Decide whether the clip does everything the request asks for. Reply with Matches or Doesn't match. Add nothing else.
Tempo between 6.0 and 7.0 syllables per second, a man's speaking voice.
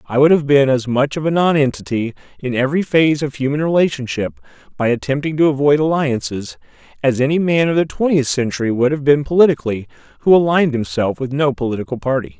Matches